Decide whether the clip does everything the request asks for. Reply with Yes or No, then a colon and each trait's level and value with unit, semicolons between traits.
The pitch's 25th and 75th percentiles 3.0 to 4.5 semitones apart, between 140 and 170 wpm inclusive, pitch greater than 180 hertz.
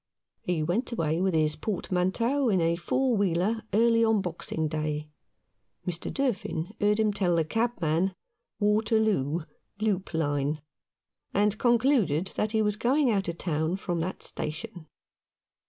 No: average, 5.2 semitones; average, 145 wpm; high, 190 Hz